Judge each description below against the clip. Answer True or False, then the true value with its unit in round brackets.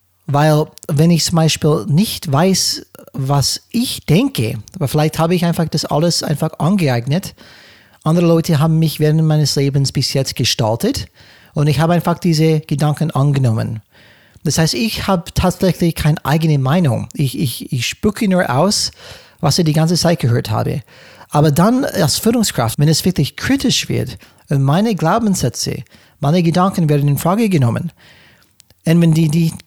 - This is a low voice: False (155 Hz)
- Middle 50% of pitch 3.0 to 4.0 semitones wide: True (3.6 semitones)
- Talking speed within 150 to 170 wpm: True (160 wpm)